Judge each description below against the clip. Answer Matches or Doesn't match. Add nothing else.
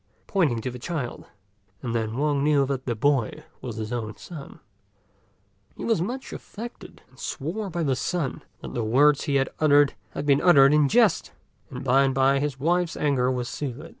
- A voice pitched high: Doesn't match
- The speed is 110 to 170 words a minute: Doesn't match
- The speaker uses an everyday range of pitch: Matches